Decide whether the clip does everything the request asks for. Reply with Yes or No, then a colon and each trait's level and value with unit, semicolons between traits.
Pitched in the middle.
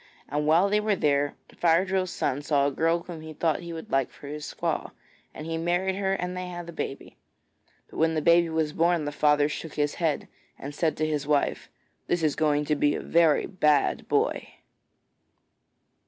Yes: medium, 160 Hz